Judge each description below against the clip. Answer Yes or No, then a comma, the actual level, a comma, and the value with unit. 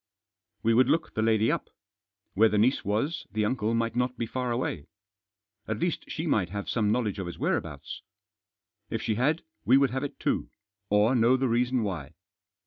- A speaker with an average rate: Yes, average, 190 wpm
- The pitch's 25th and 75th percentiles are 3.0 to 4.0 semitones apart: Yes, average, 3.3 semitones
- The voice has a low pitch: Yes, low, 115 Hz